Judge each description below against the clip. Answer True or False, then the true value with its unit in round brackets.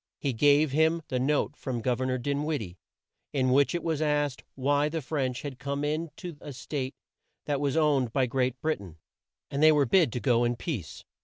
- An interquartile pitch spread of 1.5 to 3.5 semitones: True (2.8 semitones)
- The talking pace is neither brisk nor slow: False (220 wpm)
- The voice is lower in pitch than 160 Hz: True (140 Hz)